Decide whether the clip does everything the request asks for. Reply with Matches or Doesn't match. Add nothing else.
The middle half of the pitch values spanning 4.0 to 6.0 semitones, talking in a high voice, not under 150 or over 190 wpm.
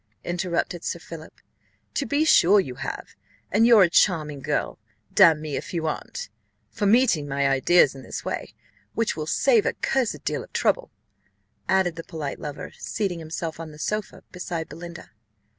Doesn't match